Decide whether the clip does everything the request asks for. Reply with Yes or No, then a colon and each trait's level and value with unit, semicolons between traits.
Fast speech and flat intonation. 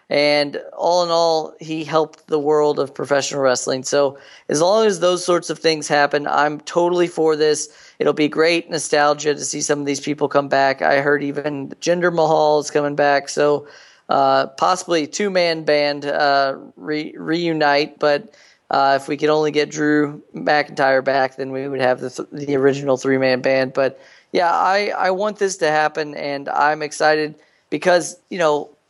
No: average, 185 wpm; narrow, 1.9 semitones